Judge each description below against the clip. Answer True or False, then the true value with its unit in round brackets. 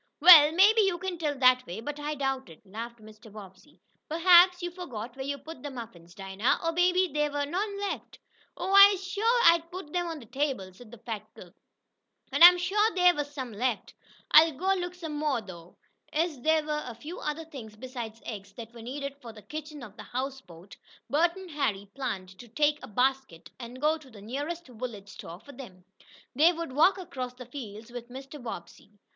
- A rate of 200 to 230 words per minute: True (205 wpm)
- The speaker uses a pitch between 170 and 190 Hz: False (275 Hz)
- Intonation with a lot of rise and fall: True (6.5 semitones)